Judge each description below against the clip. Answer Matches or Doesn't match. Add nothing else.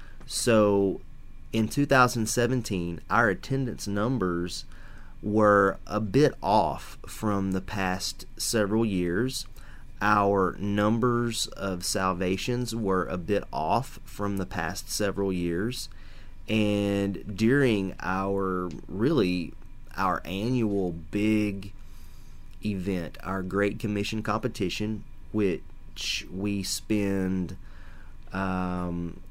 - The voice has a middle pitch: Doesn't match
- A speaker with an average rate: Doesn't match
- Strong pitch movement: Doesn't match